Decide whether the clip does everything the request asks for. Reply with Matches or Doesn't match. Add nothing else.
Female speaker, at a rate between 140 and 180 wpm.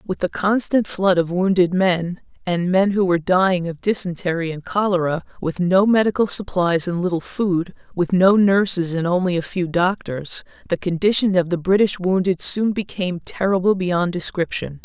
Matches